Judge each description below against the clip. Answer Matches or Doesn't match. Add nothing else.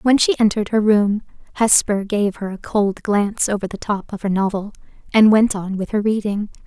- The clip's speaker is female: Matches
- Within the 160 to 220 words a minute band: Matches